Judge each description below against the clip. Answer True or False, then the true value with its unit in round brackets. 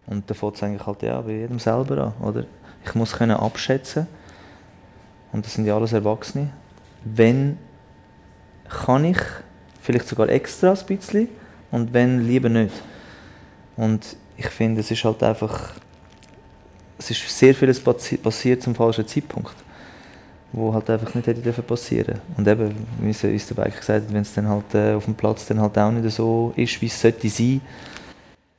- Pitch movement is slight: True (2.3 semitones)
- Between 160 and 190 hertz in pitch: False (110 Hz)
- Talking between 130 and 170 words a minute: True (160 wpm)